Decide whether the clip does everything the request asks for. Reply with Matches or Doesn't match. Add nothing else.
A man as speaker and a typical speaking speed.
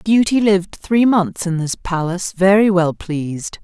Doesn't match